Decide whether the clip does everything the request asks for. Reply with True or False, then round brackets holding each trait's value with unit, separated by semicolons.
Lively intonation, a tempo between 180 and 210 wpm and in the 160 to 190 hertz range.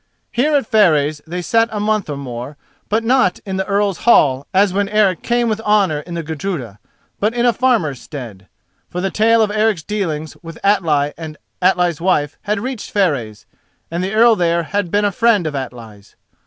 True (5.9 semitones; 195 wpm; 185 Hz)